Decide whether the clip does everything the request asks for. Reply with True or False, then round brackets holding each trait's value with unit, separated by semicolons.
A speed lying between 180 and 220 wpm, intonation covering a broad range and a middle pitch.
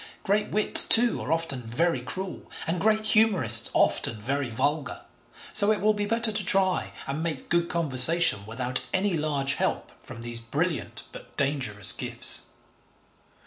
False (150 wpm; 7.4 semitones; 165 Hz)